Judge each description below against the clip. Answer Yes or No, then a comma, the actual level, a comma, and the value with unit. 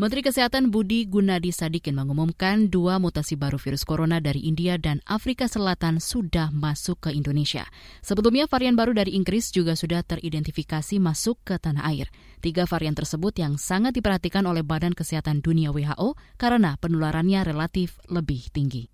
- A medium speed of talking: No, fast, 150 wpm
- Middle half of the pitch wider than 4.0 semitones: Yes, average, 4.5 semitones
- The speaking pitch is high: No, medium, 170 Hz